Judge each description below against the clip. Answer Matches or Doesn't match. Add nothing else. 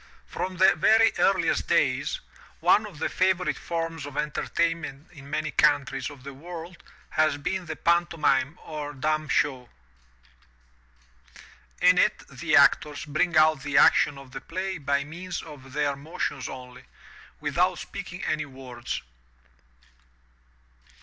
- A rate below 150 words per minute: Matches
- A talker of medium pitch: Matches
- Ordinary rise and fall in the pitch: Matches